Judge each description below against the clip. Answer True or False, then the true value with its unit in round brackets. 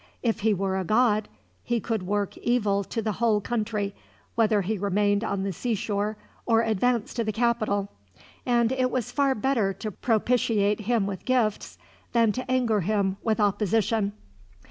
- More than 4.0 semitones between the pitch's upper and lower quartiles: False (2.7 semitones)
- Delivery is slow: False (165 wpm)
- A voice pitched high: True (215 Hz)